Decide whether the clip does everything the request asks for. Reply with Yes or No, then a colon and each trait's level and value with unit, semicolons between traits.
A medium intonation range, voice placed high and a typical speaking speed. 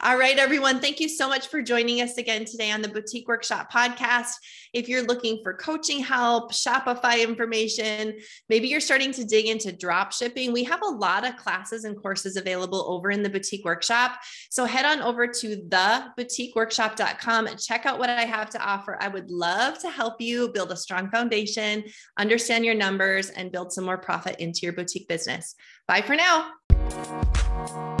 Yes: average, 4.0 semitones; high, 225 Hz; average, 185 wpm